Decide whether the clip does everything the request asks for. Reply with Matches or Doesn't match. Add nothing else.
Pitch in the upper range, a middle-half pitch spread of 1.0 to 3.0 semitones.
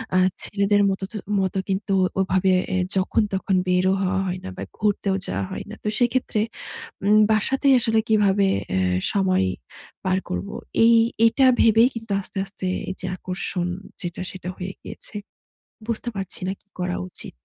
Matches